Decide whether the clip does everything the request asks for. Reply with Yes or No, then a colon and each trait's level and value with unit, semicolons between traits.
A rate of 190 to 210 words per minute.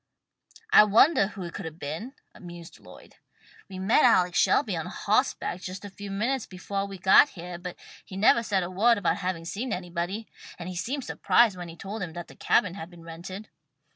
Yes: average, 200 wpm